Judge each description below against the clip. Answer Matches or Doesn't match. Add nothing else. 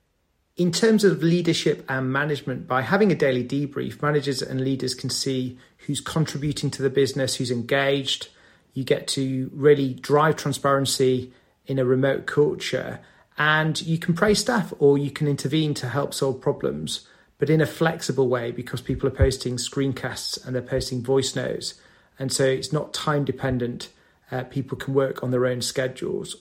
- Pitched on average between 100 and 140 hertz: Matches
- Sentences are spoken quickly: Doesn't match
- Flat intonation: Matches